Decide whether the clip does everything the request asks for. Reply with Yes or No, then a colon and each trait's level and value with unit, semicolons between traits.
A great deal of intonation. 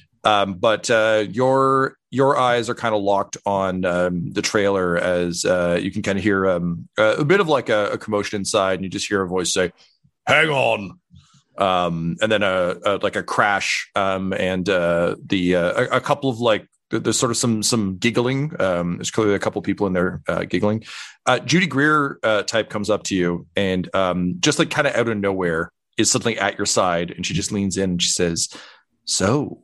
No: average, 4.4 semitones